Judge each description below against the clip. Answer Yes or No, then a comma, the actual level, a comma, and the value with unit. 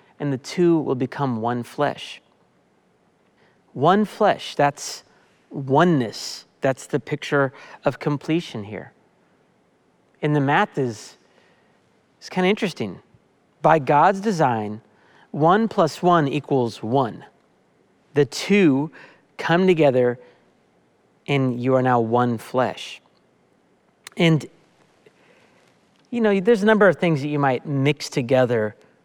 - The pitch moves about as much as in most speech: Yes, average, 4.8 semitones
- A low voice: No, medium, 145 Hz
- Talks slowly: Yes, slow, 115 wpm